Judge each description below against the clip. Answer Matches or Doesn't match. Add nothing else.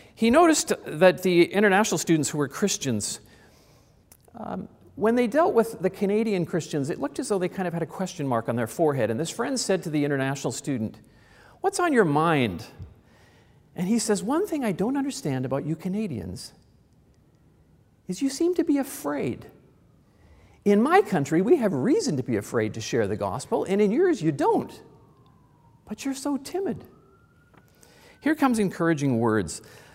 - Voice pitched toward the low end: Doesn't match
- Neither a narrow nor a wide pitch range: Doesn't match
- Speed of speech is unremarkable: Matches